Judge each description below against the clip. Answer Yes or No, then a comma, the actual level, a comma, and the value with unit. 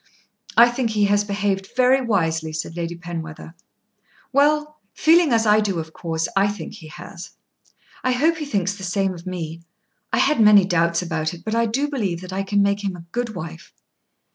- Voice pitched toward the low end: No, high, 200 Hz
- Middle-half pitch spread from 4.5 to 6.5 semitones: Yes, average, 5.3 semitones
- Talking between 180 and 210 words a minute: Yes, average, 195 wpm